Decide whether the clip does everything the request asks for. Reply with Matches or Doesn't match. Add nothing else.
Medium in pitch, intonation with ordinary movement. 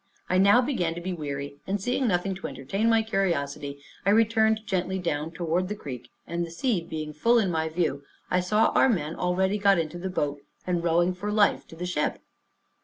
Matches